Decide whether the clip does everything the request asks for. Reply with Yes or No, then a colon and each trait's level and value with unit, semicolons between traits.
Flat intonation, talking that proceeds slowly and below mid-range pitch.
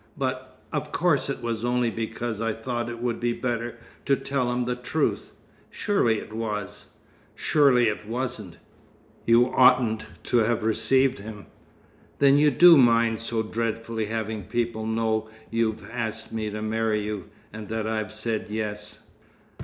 No: narrow, 1.8 semitones; average, 155 wpm; low, 115 Hz